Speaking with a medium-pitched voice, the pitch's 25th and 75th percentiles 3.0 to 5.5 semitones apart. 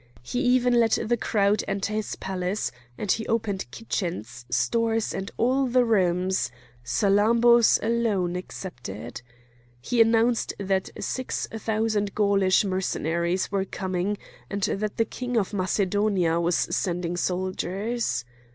No: high, 200 Hz; average, 3.9 semitones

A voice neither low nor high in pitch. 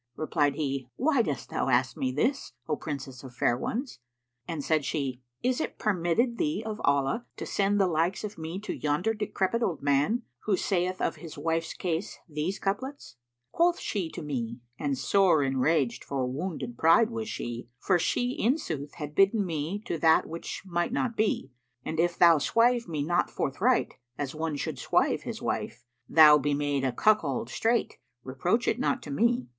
Yes: medium, 165 Hz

